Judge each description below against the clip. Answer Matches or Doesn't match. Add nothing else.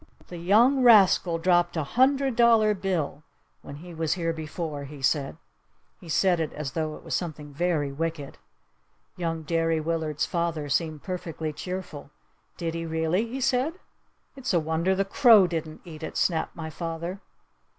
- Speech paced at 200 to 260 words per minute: Doesn't match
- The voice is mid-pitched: Matches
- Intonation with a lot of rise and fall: Doesn't match